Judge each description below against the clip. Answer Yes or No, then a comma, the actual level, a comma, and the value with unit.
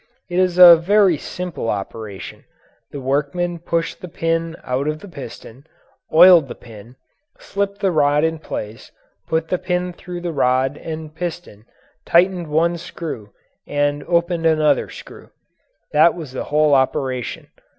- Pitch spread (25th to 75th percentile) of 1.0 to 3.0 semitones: No, average, 4.0 semitones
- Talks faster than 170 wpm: No, average, 145 wpm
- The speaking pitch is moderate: Yes, medium, 160 Hz